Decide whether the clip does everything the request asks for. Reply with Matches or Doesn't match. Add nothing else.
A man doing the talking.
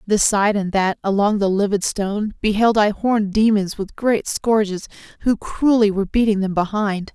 Doesn't match